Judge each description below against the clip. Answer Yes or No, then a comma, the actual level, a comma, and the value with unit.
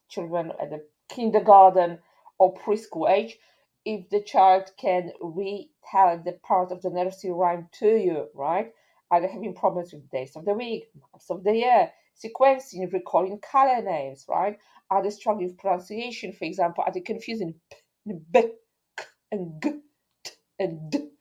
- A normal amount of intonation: Yes, average, 3.7 semitones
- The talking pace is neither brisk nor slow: Yes, average, 160 wpm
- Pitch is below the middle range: No, high, 190 Hz